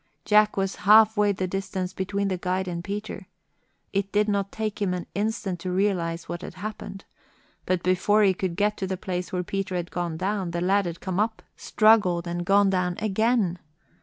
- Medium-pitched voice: No, high, 195 Hz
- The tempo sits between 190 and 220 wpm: Yes, average, 195 wpm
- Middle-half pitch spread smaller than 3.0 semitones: Yes, narrow, 2.4 semitones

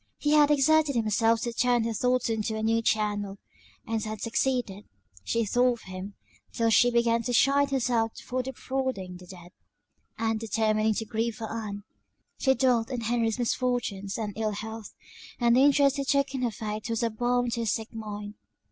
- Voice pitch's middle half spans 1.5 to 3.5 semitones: Yes, narrow, 2.5 semitones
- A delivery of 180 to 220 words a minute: Yes, average, 185 wpm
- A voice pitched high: Yes, high, 230 Hz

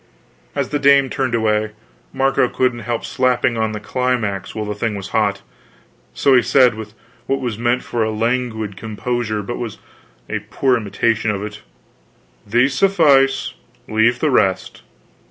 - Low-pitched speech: Yes, low, 120 Hz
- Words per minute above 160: No, average, 155 wpm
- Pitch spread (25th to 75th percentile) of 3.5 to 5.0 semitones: No, average, 3.0 semitones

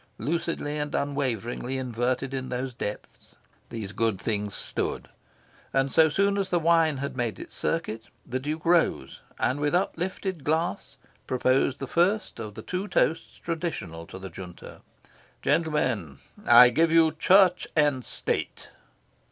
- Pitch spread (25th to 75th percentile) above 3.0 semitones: Yes, wide, 5.5 semitones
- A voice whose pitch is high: No, medium, 140 Hz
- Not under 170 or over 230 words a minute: No, average, 145 wpm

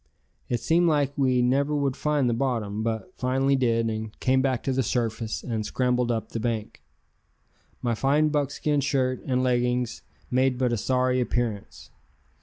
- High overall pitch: No, low, 125 Hz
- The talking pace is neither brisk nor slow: Yes, average, 165 wpm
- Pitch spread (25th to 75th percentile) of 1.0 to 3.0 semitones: Yes, narrow, 2.6 semitones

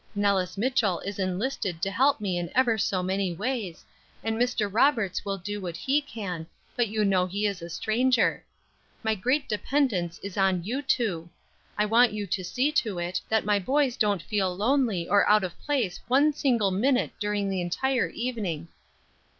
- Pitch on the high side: Yes, high, 205 Hz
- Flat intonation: No, average, 4.8 semitones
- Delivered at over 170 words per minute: Yes, average, 180 wpm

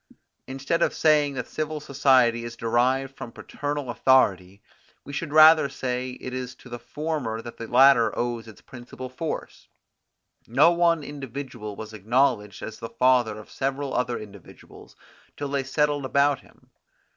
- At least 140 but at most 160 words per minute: Yes, average, 155 wpm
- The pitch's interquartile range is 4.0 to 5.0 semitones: No, average, 3.4 semitones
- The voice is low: Yes, low, 130 Hz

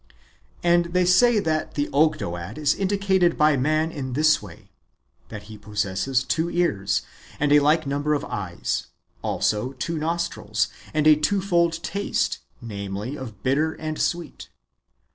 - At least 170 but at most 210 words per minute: No, average, 140 wpm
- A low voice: No, medium, 150 Hz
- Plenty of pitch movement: Yes, wide, 6.7 semitones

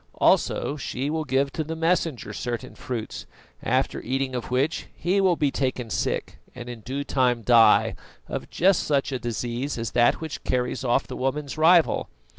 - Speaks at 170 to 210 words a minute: Yes, average, 175 wpm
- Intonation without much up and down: No, average, 3.8 semitones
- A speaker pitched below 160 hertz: Yes, low, 135 Hz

